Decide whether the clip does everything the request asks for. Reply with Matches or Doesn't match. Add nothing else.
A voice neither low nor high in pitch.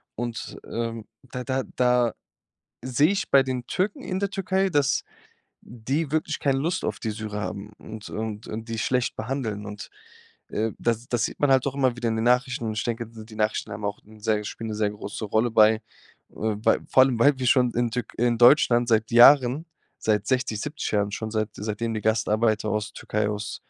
Doesn't match